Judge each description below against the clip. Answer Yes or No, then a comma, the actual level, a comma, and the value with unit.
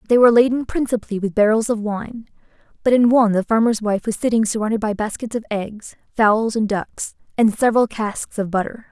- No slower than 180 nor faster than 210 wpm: Yes, average, 195 wpm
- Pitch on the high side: Yes, high, 220 Hz